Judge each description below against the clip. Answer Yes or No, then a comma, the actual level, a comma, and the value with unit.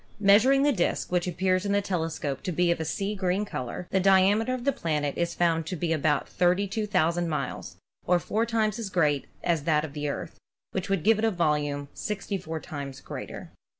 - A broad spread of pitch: No, average, 4.2 semitones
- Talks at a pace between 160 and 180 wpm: No, average, 200 wpm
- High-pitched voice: No, medium, 180 Hz